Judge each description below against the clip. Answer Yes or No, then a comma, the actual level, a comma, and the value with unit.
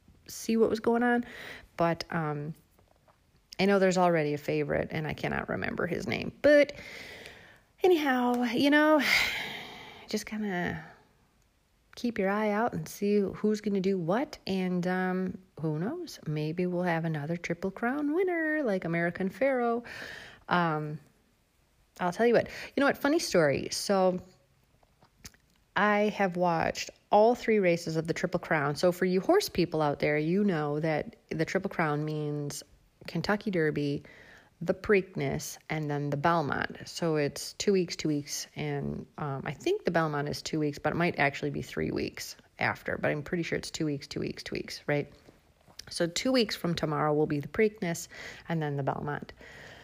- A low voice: No, medium, 180 Hz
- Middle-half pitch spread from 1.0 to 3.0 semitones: No, wide, 5.4 semitones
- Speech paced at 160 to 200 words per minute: Yes, average, 170 wpm